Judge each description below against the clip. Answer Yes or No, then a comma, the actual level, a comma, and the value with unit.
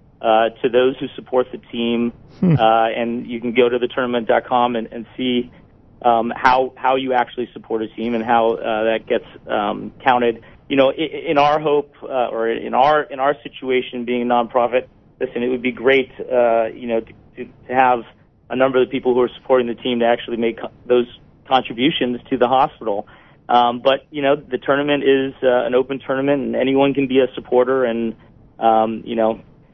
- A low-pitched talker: Yes, low, 125 Hz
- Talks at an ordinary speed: No, fast, 210 wpm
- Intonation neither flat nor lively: No, narrow, 2.2 semitones